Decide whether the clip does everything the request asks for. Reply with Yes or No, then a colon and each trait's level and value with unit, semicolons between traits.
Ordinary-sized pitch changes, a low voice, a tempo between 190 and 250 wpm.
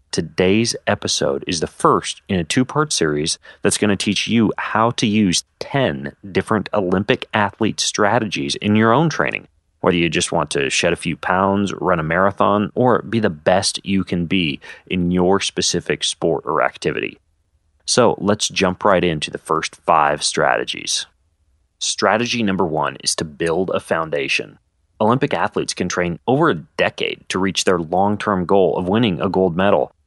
No: average, 4.2 semitones; very low, 95 Hz; average, 175 wpm